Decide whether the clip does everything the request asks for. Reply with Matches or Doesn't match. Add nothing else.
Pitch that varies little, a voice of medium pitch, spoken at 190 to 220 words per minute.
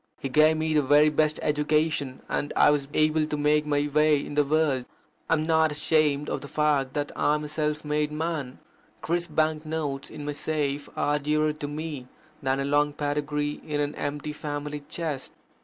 Matches